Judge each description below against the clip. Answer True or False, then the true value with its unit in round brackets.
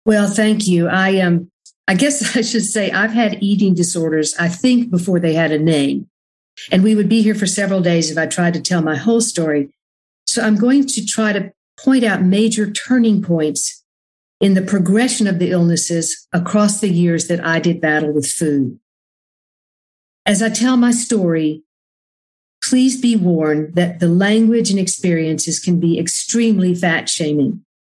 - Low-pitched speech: False (185 Hz)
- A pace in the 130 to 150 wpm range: False (175 wpm)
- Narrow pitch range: False (4.8 semitones)